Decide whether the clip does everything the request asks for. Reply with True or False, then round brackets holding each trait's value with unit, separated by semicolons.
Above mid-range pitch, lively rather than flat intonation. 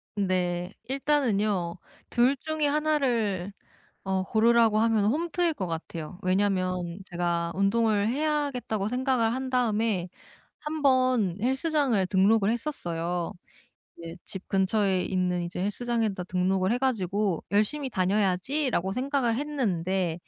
True (210 Hz; 5.7 semitones)